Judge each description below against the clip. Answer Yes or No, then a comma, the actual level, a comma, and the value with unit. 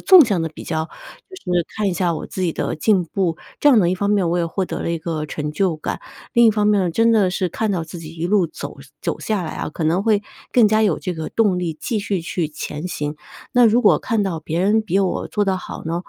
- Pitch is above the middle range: No, medium, 180 Hz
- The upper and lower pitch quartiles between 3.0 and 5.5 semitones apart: Yes, average, 4.2 semitones